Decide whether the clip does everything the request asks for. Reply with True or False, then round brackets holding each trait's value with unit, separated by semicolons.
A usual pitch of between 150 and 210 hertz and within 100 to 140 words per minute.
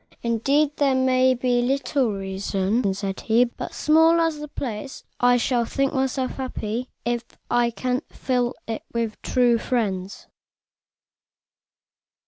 False (245 Hz; 135 wpm)